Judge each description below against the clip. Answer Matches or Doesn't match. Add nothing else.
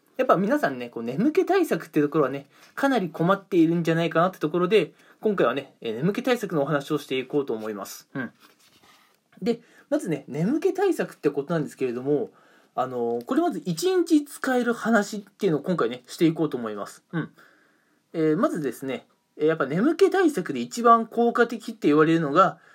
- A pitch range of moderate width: Doesn't match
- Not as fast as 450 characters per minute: Matches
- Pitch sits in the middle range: Matches